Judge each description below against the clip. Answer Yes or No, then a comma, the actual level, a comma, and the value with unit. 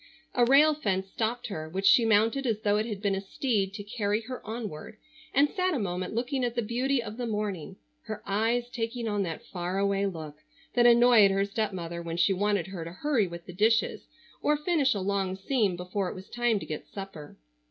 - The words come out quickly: Yes, fast, 215 wpm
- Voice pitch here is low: No, high, 210 Hz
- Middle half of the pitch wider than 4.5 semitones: No, average, 3.9 semitones